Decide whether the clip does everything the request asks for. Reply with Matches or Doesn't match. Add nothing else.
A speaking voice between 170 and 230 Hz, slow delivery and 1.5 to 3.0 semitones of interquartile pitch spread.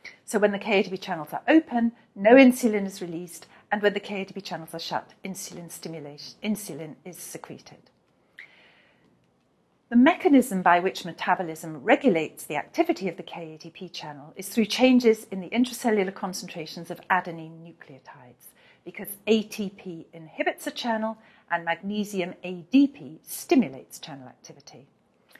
Doesn't match